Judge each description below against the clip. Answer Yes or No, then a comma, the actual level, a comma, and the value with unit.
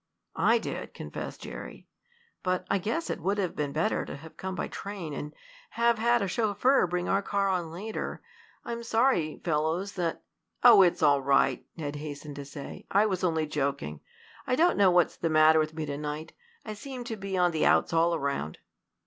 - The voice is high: No, medium, 175 Hz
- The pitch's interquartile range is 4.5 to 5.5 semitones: Yes, average, 4.9 semitones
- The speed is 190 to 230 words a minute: Yes, average, 200 wpm